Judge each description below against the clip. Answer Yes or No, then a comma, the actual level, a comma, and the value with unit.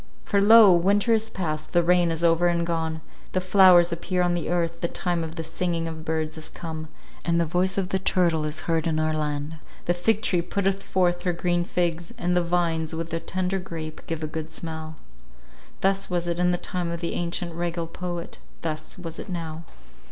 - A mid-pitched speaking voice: Yes, medium, 170 Hz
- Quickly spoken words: Yes, fast, 210 wpm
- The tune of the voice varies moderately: No, narrow, 1.8 semitones